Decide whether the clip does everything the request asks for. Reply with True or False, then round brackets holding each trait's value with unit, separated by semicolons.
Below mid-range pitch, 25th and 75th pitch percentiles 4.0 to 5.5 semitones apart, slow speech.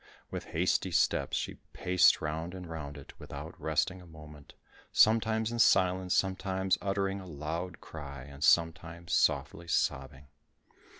False (85 Hz; 3.6 semitones; 130 wpm)